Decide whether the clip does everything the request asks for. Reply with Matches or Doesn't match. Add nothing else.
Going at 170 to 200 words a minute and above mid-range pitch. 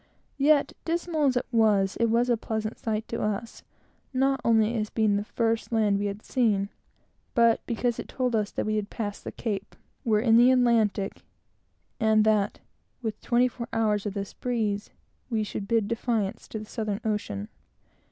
Matches